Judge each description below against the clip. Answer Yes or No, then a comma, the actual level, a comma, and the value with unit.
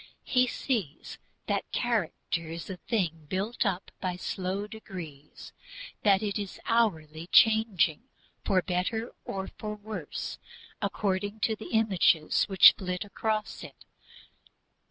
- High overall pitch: Yes, high, 195 Hz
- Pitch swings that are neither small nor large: Yes, average, 3.3 semitones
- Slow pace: Yes, slow, 120 wpm